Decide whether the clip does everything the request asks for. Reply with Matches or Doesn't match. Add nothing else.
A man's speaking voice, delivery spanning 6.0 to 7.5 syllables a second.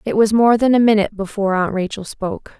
Doesn't match